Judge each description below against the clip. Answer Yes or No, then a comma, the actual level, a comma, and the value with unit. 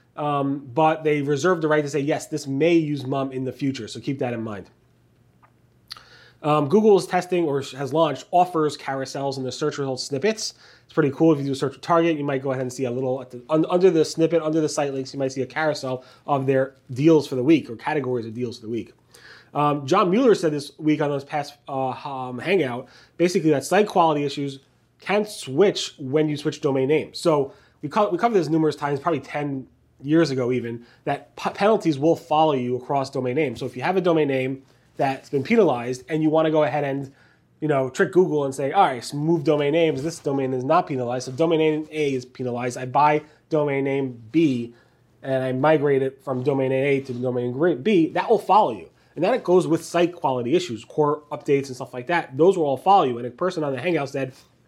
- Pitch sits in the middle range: Yes, medium, 145 Hz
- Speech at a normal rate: No, fast, 235 wpm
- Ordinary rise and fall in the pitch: Yes, average, 3.3 semitones